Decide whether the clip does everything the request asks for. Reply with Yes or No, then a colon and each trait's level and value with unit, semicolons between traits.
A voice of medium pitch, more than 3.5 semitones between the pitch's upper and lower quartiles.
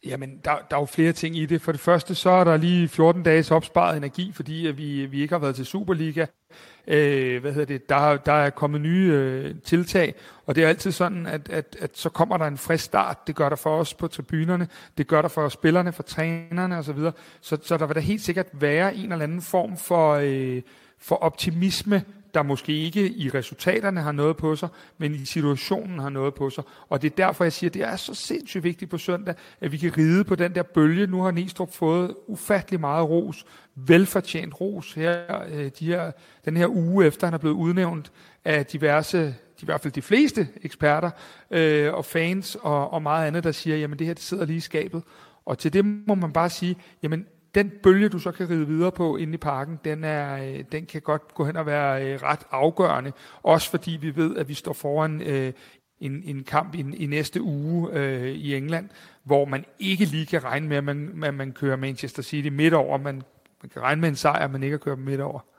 No: medium, 160 Hz; average, 3.0 semitones